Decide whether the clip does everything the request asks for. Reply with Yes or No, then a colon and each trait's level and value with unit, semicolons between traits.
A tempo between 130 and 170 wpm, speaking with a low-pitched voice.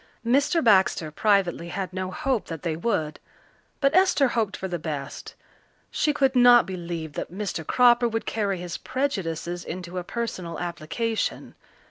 No: average, 150 wpm; high, 190 Hz